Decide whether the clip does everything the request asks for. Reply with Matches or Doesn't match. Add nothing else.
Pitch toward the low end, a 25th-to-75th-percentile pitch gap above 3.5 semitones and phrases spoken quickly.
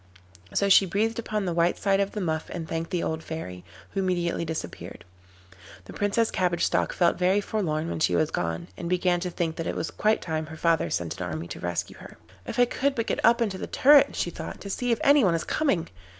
Doesn't match